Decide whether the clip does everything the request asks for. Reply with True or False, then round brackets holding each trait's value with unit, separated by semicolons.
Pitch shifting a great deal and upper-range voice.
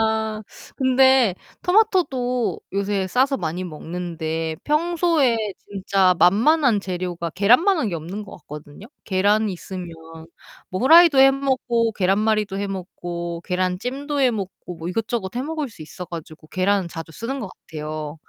True (6.5 semitones; 200 Hz)